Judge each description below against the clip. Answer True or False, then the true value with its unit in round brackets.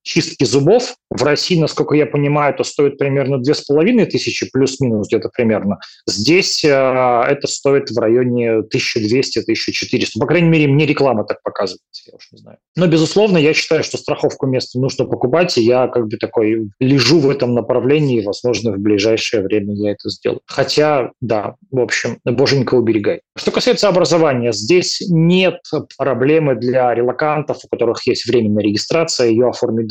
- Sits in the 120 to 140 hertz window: True (135 Hz)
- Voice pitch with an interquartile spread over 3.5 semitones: True (4.2 semitones)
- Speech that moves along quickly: True (165 wpm)